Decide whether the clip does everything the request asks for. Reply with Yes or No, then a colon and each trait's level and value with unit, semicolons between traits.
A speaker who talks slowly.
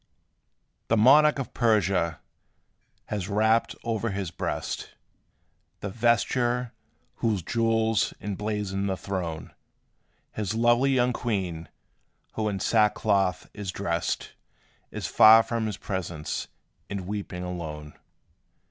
Yes: slow, 105 wpm